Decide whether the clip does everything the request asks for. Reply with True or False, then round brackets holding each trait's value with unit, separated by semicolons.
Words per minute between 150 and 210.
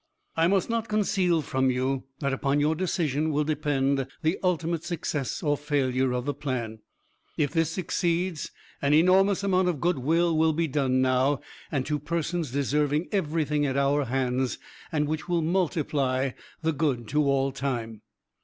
True (160 wpm)